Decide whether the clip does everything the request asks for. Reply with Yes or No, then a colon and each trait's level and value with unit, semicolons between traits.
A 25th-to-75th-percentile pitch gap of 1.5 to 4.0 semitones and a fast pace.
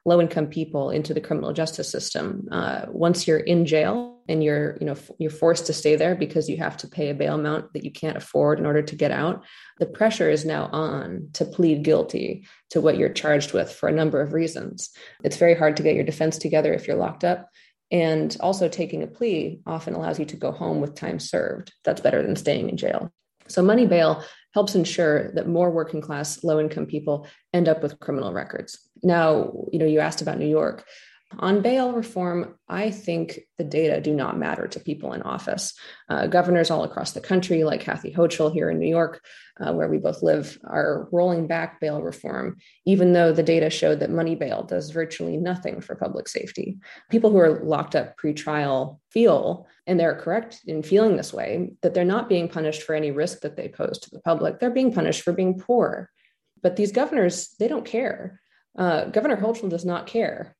Yes: average, 3.0 semitones; fast, 210 wpm